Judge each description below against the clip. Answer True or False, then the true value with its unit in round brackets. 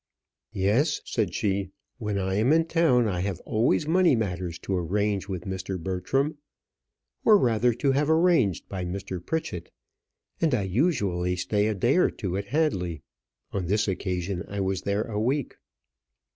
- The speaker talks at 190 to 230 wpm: False (160 wpm)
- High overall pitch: False (100 Hz)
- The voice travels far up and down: True (5.8 semitones)